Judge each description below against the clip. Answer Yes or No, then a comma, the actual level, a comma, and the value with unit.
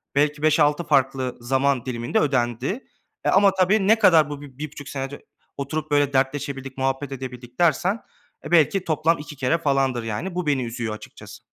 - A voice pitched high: No, medium, 140 Hz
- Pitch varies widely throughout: No, average, 3.0 semitones